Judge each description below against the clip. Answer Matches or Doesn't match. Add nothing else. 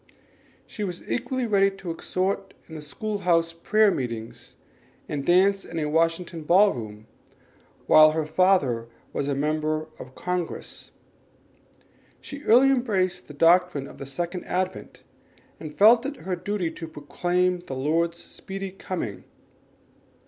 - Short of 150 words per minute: Matches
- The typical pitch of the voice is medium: Matches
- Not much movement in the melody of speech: Doesn't match